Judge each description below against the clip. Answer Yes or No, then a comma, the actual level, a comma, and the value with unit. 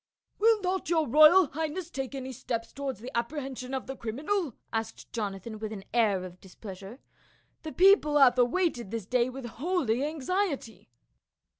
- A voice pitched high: Yes, very high, 260 Hz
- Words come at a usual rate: Yes, average, 170 wpm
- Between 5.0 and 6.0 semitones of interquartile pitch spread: Yes, wide, 5.6 semitones